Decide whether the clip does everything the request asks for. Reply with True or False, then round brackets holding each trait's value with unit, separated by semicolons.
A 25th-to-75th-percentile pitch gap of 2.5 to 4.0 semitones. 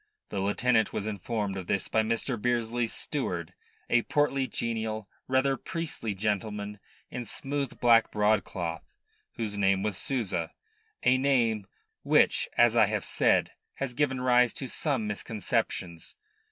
True (3.6 semitones)